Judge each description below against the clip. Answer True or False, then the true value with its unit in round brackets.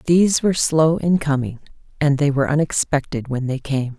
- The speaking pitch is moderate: True (145 Hz)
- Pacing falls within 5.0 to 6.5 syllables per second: True (5.5 syllables/s)